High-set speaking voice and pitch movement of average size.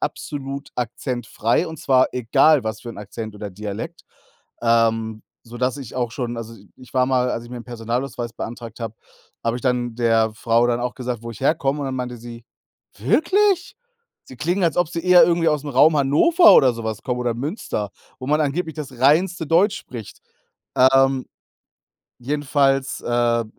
No: low, 125 Hz; average, 4.0 semitones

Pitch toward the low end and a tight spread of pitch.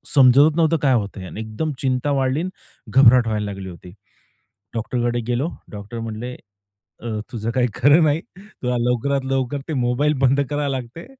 No: low, 125 Hz; average, 3.4 semitones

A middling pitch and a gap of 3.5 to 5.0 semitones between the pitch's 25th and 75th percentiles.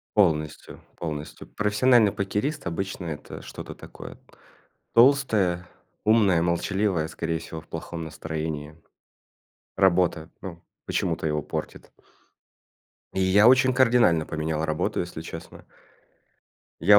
No: very low, 85 Hz; average, 4.5 semitones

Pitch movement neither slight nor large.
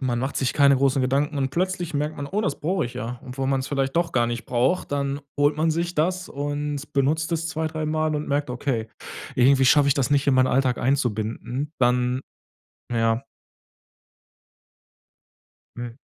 Yes: average, 3.1 semitones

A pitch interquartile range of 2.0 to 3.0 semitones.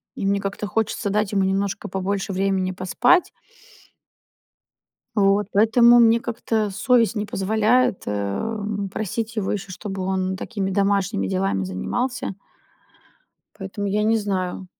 Yes: narrow, 2.4 semitones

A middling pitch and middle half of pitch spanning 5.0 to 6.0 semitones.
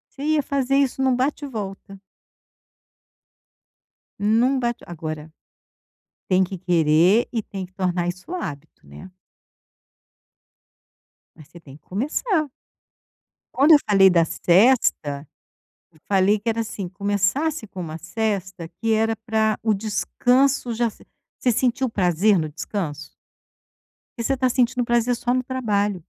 No: high, 210 Hz; wide, 5.5 semitones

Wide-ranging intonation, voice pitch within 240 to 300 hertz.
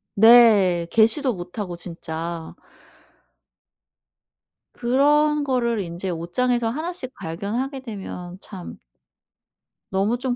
No: wide, 6.3 semitones; high, 220 Hz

